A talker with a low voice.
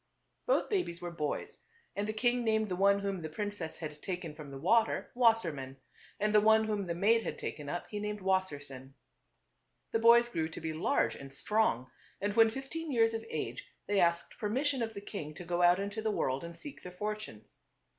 No: high, 200 Hz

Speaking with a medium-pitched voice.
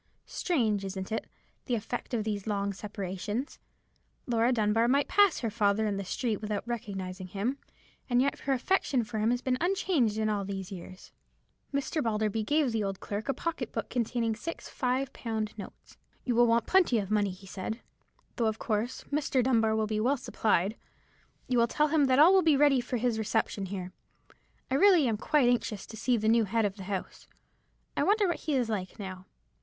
No: high, 225 Hz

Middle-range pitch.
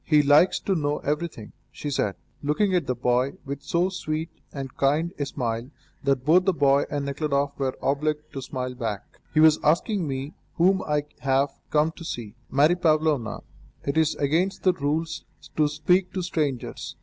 Yes: medium, 150 Hz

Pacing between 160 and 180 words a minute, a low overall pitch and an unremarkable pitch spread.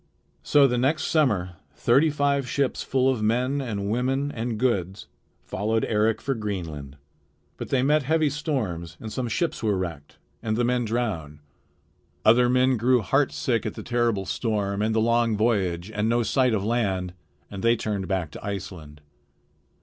Yes: average, 165 wpm; low, 115 Hz; average, 4.3 semitones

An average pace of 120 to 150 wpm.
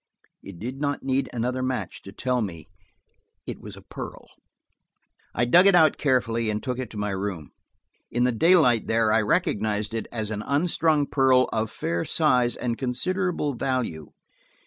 No: average, 170 wpm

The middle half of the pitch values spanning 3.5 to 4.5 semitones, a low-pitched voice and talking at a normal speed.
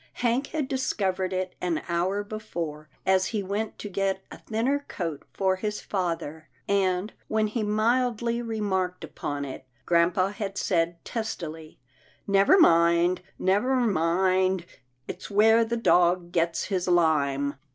No: average, 4.0 semitones; high, 190 Hz; average, 145 wpm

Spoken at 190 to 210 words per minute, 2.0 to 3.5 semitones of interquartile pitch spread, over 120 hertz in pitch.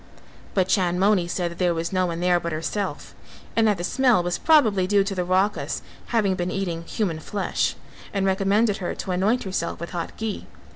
Yes: average, 195 wpm; average, 2.7 semitones; high, 190 Hz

